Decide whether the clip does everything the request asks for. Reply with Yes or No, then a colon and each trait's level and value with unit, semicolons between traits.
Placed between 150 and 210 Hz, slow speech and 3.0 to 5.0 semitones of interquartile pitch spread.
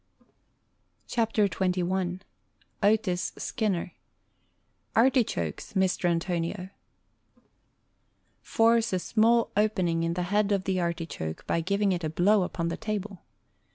Yes: medium, 185 Hz; slow, 125 wpm; average, 3.6 semitones